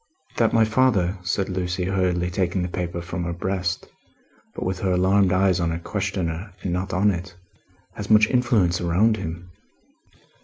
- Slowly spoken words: No, average, 165 wpm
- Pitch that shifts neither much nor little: No, narrow, 2.0 semitones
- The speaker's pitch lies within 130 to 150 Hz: No, very low, 90 Hz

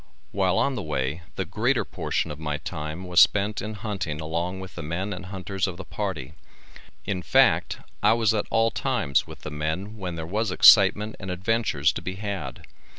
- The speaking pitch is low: Yes, very low, 95 Hz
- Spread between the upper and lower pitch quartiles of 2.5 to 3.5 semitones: No, average, 4.6 semitones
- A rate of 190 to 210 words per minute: Yes, average, 195 wpm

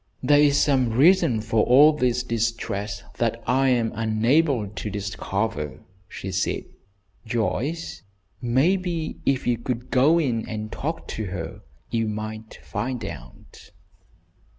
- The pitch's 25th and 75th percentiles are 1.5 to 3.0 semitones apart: No, average, 4.0 semitones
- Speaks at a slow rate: Yes, slow, 130 wpm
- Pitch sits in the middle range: No, low, 115 Hz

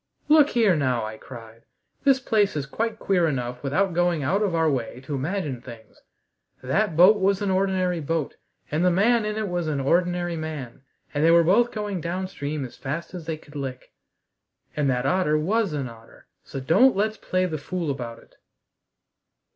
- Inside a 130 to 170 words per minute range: No, average, 185 wpm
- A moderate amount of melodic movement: No, wide, 5.9 semitones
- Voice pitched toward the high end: No, medium, 165 Hz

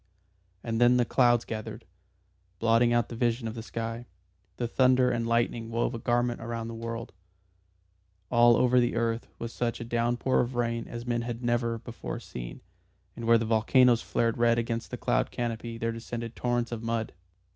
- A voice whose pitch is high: No, low, 115 Hz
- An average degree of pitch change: No, narrow, 0.7 semitones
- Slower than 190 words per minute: Yes, average, 180 wpm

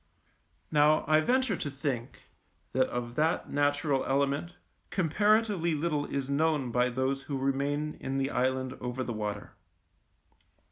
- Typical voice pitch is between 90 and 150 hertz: Yes, medium, 140 Hz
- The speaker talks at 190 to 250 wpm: No, slow, 135 wpm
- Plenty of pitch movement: No, average, 3.0 semitones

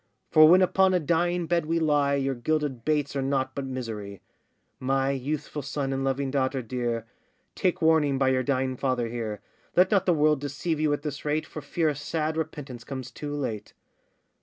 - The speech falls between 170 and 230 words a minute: Yes, average, 190 wpm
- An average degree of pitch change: Yes, average, 3.0 semitones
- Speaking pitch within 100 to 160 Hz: Yes, medium, 140 Hz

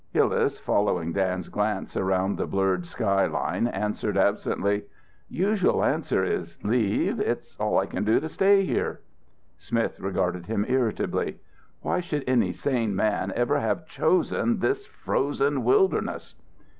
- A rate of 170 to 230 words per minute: No, slow, 135 wpm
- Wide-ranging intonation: Yes, wide, 7.0 semitones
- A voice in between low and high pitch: No, low, 105 Hz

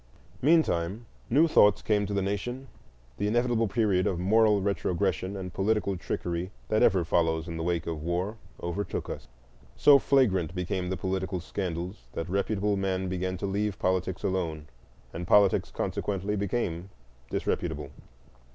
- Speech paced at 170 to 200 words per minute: No, average, 145 wpm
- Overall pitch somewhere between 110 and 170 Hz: No, very low, 95 Hz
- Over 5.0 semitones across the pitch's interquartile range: No, average, 2.9 semitones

